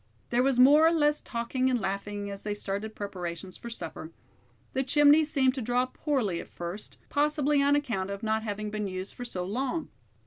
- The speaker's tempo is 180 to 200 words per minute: Yes, average, 195 wpm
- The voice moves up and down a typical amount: No, wide, 5.8 semitones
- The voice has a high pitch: Yes, high, 235 Hz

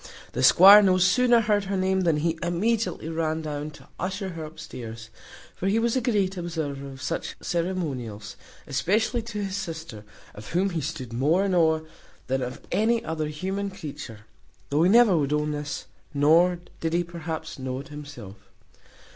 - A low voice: No, medium, 165 Hz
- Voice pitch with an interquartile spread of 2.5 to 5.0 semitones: Yes, average, 4.7 semitones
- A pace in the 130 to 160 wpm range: No, average, 170 wpm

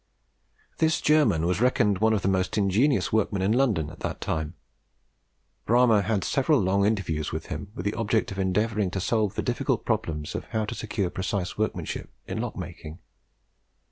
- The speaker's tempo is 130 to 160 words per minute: No, average, 175 wpm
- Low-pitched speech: Yes, low, 105 Hz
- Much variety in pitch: No, average, 3.4 semitones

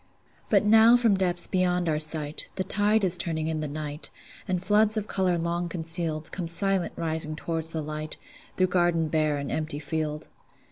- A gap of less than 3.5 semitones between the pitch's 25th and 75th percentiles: Yes, average, 3.1 semitones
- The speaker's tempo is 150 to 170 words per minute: No, average, 180 wpm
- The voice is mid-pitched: Yes, medium, 170 Hz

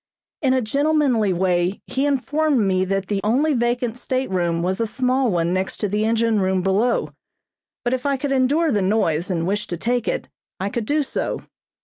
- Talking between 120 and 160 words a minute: No, average, 190 wpm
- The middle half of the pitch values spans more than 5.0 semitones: Yes, wide, 5.5 semitones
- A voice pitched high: Yes, high, 225 Hz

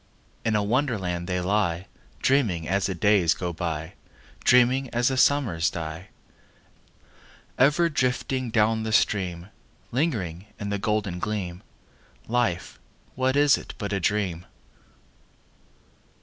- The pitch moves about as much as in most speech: No, wide, 5.7 semitones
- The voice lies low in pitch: Yes, low, 105 Hz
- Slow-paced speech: Yes, slow, 120 wpm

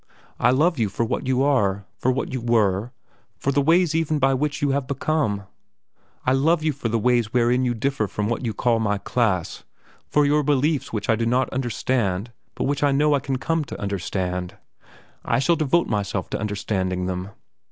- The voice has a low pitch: Yes, low, 125 Hz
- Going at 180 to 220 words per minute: Yes, average, 200 wpm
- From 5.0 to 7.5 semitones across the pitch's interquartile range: Yes, average, 5.3 semitones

